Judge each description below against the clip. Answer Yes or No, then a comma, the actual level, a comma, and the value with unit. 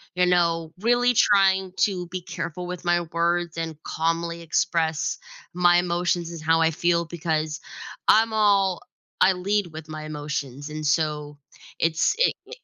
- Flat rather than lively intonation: Yes, narrow, 2.3 semitones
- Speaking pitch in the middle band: Yes, medium, 170 Hz